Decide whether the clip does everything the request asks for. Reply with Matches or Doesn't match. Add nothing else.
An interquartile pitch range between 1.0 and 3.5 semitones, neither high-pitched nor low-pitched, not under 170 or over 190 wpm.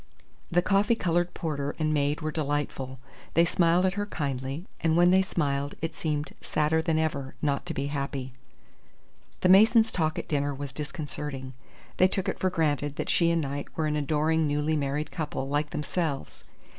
Matches